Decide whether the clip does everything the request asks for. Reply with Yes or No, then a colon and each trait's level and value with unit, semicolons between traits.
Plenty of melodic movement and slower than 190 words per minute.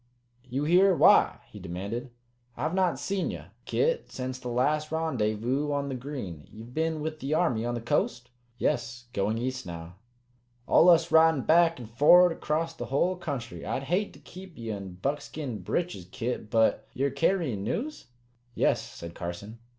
Yes: wide, 6.1 semitones; average, 165 wpm